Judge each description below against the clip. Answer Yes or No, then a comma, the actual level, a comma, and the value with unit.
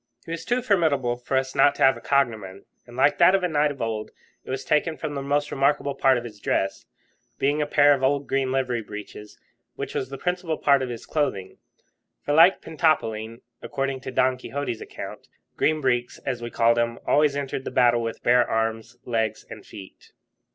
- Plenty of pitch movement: No, average, 3.7 semitones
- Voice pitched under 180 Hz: Yes, low, 135 Hz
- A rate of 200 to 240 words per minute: Yes, fast, 205 wpm